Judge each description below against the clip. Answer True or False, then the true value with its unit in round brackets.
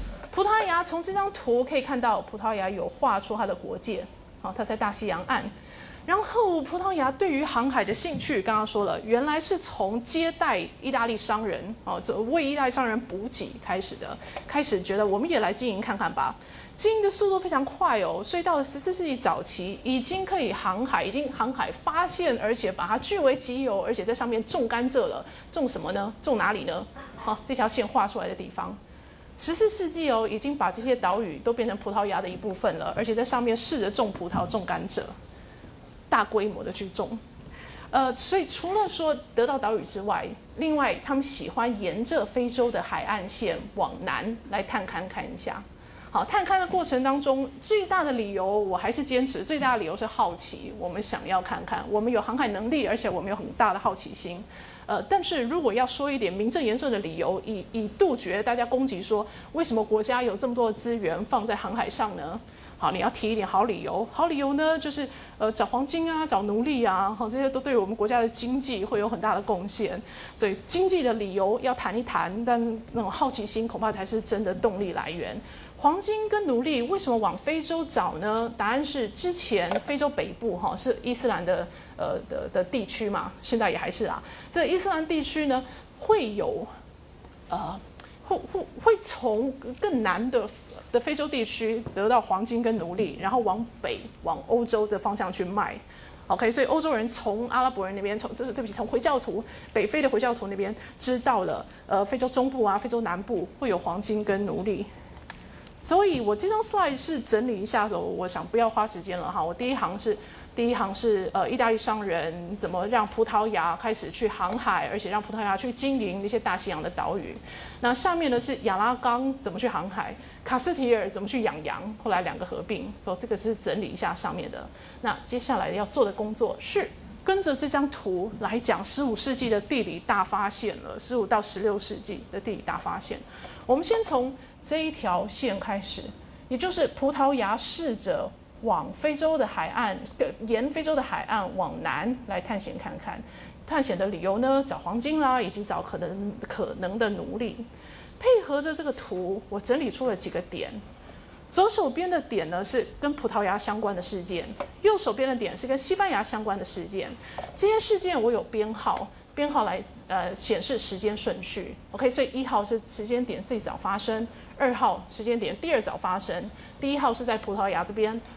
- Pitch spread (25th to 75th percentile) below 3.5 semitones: False (5.0 semitones)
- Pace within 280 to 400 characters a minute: True (295 characters per minute)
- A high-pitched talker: True (240 Hz)